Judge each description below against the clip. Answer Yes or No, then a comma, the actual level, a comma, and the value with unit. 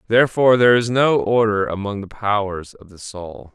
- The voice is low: Yes, low, 105 Hz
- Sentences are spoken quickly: No, average, 185 wpm